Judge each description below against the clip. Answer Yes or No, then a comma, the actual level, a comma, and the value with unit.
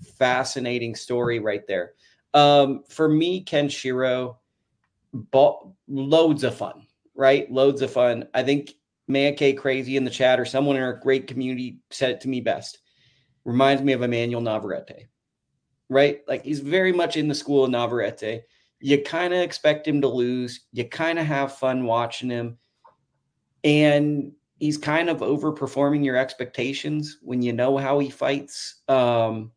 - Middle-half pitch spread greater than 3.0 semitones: No, narrow, 2.6 semitones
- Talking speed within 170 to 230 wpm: No, average, 160 wpm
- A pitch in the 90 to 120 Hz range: No, low, 135 Hz